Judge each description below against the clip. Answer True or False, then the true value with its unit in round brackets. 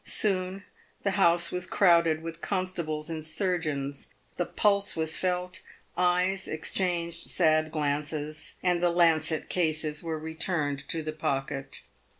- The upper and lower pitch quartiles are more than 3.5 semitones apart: False (2.6 semitones)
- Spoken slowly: True (130 wpm)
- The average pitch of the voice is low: False (165 Hz)